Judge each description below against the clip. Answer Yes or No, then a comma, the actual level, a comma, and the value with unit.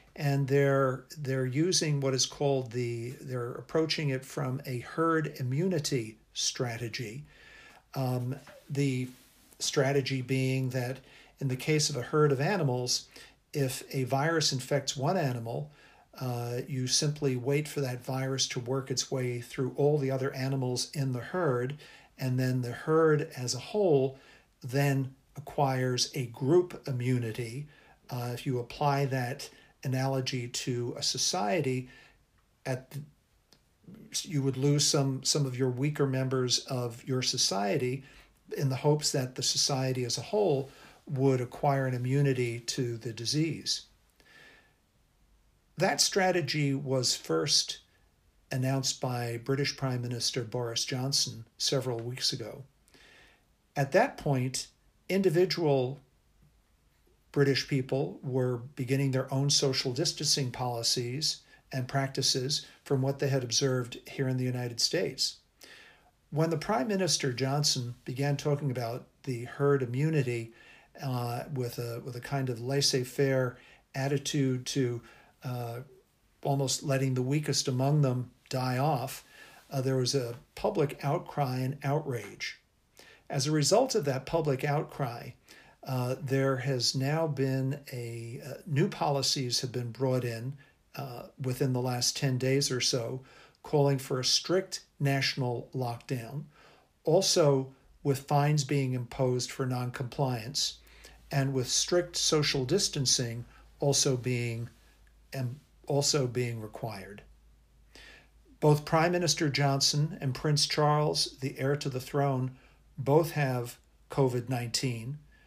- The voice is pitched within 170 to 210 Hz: No, low, 135 Hz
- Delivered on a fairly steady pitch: Yes, narrow, 2.2 semitones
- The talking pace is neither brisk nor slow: No, slow, 130 wpm